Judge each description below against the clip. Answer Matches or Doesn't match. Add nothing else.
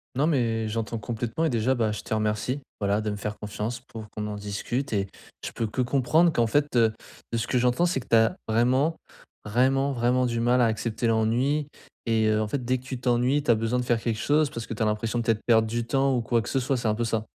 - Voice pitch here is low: Matches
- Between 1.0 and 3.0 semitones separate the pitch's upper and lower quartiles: Matches